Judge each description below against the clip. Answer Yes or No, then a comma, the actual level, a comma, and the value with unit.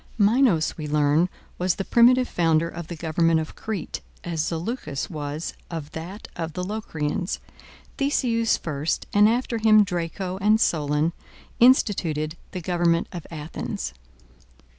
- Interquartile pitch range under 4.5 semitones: No, average, 5.0 semitones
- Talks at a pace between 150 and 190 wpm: No, slow, 135 wpm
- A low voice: No, medium, 170 Hz